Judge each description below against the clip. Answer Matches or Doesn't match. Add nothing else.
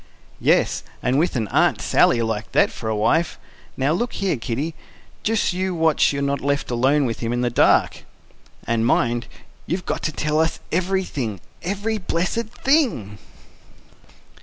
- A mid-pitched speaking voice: Matches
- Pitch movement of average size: Doesn't match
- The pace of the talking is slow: Doesn't match